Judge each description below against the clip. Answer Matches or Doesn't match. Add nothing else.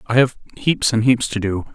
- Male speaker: Matches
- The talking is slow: Doesn't match